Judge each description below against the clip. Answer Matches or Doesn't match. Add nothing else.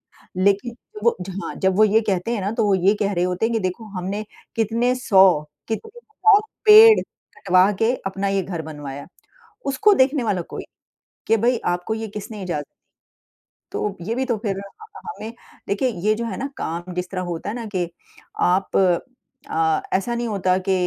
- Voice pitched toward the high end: Matches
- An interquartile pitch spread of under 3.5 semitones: Doesn't match